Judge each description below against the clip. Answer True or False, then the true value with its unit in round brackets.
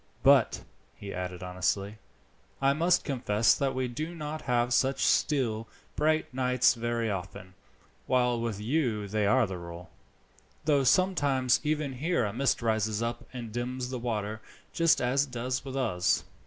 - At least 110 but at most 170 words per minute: True (155 wpm)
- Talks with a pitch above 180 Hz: False (125 Hz)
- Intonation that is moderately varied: True (4.1 semitones)